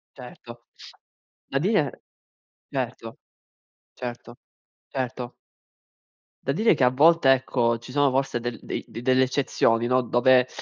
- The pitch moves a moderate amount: No, narrow, 2.2 semitones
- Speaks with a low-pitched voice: Yes, low, 130 Hz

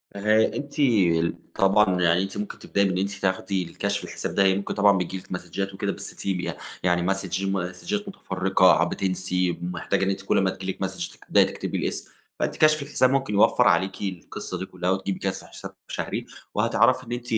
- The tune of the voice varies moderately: No, narrow, 1.5 semitones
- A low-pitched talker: Yes, very low, 95 Hz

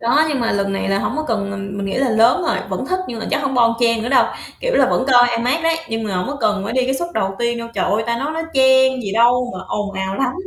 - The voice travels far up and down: No, average, 4.3 semitones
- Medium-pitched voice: No, high, 235 Hz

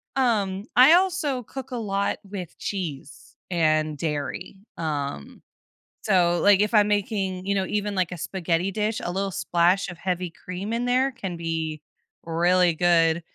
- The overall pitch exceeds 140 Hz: Yes, medium, 185 Hz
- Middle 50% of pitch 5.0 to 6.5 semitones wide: No, average, 3.7 semitones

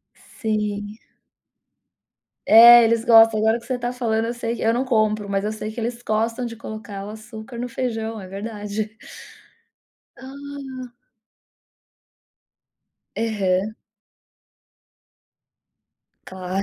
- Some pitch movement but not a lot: No, narrow, 2.0 semitones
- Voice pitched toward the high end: Yes, high, 225 Hz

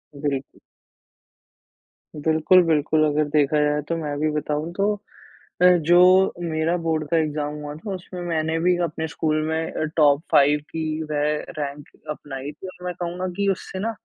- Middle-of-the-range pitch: Yes, medium, 155 Hz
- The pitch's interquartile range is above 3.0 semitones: No, narrow, 2.6 semitones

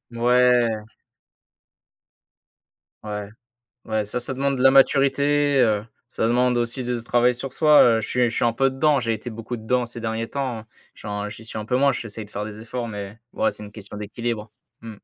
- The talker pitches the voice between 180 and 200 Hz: No, low, 115 Hz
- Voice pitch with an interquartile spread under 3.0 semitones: Yes, narrow, 2.5 semitones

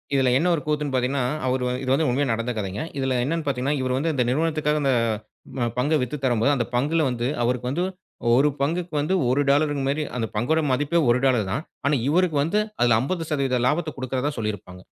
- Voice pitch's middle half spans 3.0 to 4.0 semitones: Yes, average, 3.4 semitones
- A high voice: No, low, 135 Hz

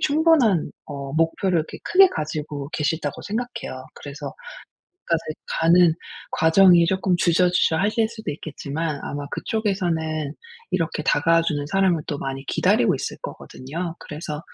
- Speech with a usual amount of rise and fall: Yes, average, 4.0 semitones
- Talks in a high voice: No, medium, 165 Hz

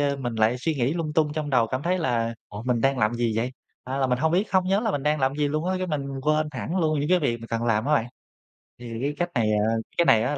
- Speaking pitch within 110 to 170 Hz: Yes, medium, 140 Hz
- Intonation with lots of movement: No, average, 4.5 semitones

